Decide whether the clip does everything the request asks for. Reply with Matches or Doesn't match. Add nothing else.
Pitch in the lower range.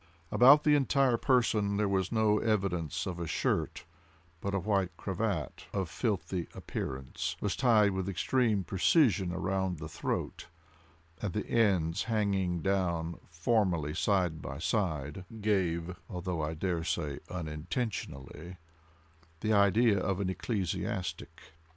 Matches